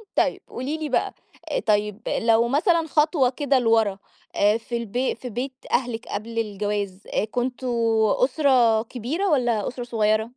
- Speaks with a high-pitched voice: Yes, high, 240 Hz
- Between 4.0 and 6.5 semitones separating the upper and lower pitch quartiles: No, average, 3.3 semitones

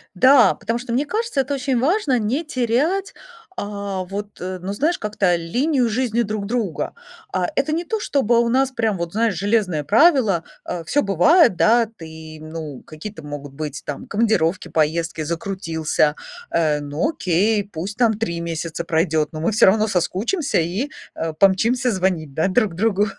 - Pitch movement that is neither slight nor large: No, wide, 6.4 semitones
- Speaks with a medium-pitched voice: No, high, 200 Hz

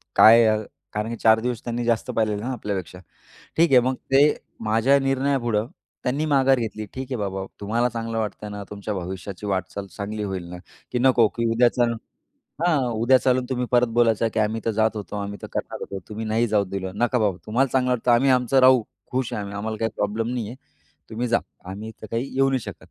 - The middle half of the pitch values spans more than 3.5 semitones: No, average, 3.1 semitones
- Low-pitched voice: Yes, low, 115 Hz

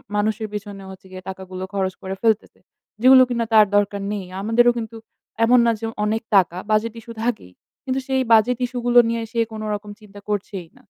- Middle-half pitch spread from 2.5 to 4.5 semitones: Yes, average, 2.9 semitones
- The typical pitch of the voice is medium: No, high, 215 Hz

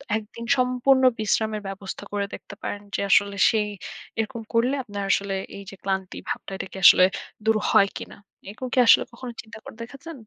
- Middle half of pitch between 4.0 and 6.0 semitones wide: No, average, 3.4 semitones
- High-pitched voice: Yes, high, 220 Hz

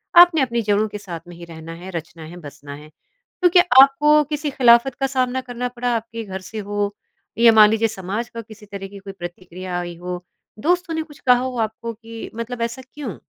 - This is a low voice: No, high, 225 Hz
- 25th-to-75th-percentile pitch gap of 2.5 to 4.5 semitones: No, average, 5.3 semitones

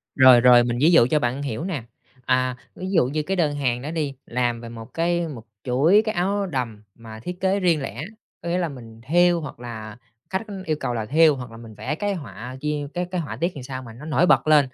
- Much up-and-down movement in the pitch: Yes, wide, 5.9 semitones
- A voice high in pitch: No, medium, 140 Hz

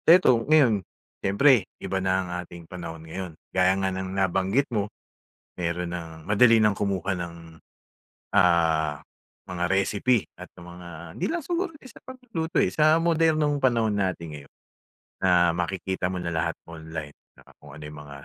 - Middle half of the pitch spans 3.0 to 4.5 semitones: No, wide, 5.6 semitones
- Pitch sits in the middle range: No, very low, 95 Hz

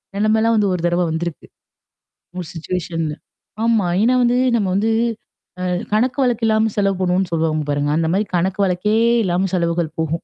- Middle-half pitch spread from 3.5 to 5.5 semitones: Yes, average, 4.4 semitones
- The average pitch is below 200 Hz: Yes, medium, 185 Hz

